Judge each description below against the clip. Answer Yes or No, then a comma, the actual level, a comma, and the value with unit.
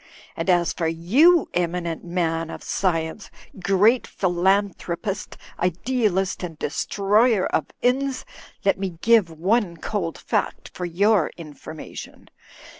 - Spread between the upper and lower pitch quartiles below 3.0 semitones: No, average, 3.8 semitones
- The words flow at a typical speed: No, slow, 115 wpm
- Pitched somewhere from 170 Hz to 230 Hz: Yes, medium, 185 Hz